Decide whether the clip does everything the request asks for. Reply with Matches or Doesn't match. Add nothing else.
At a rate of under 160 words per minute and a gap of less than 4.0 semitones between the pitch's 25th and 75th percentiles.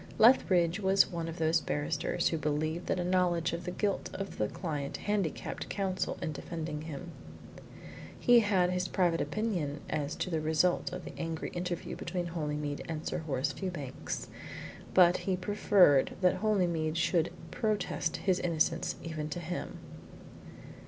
Matches